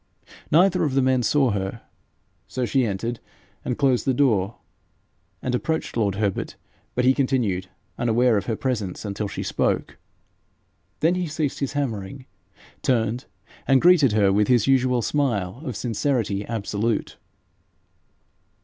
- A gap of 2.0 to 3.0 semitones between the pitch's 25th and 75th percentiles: No, average, 4.5 semitones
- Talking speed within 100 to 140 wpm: Yes, slow, 135 wpm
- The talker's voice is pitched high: No, low, 120 Hz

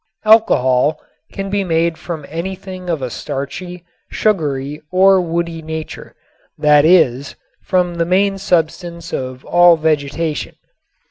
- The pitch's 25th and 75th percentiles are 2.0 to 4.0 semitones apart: Yes, average, 3.5 semitones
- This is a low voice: No, medium, 170 Hz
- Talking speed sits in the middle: No, slow, 120 wpm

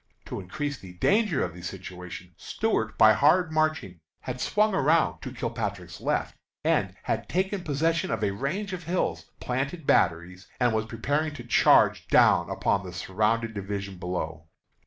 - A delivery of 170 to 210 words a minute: No, average, 155 wpm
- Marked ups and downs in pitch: Yes, wide, 8.8 semitones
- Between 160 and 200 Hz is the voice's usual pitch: No, low, 115 Hz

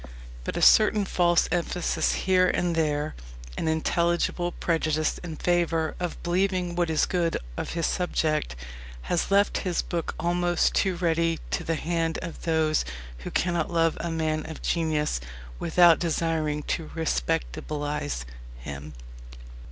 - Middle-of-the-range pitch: Yes, medium, 165 Hz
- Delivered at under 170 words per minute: Yes, slow, 135 wpm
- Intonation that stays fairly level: Yes, narrow, 2.0 semitones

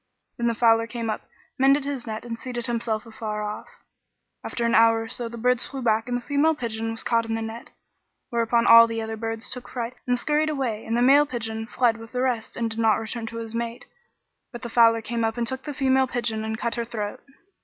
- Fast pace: Yes, fast, 240 wpm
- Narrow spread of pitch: Yes, narrow, 1.6 semitones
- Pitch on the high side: Yes, high, 230 Hz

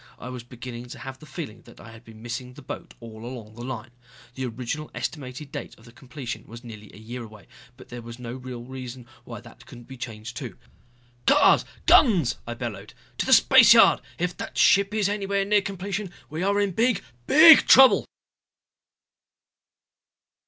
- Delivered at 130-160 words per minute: No, average, 180 wpm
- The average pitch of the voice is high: No, low, 125 Hz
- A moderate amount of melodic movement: No, wide, 6.7 semitones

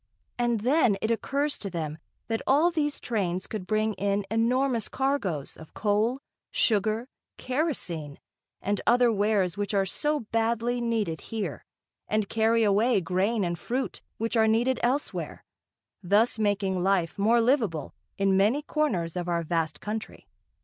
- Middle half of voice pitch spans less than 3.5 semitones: No, average, 3.8 semitones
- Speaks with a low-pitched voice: No, high, 215 Hz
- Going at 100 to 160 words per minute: Yes, average, 145 wpm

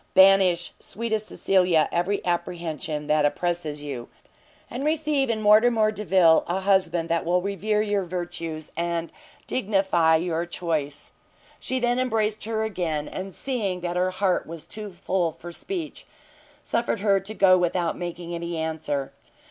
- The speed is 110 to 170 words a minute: Yes, average, 145 wpm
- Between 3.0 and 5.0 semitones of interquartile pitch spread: Yes, average, 4.0 semitones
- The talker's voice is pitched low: No, medium, 180 Hz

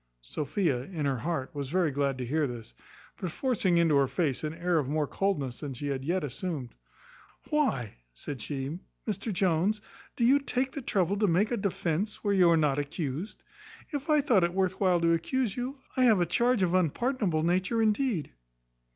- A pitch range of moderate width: No, wide, 6.2 semitones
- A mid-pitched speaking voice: Yes, medium, 175 Hz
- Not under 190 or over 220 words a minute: Yes, average, 195 wpm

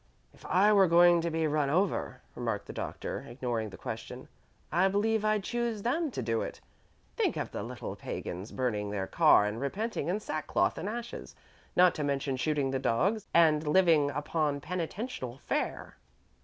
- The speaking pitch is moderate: Yes, medium, 160 Hz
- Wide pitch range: Yes, wide, 7.1 semitones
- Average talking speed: Yes, average, 170 wpm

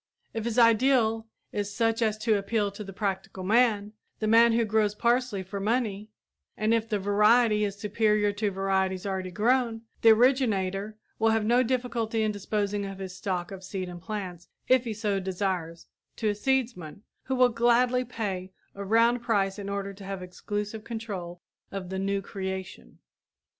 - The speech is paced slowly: No, average, 175 wpm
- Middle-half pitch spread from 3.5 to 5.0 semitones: No, average, 2.8 semitones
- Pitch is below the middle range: No, high, 210 Hz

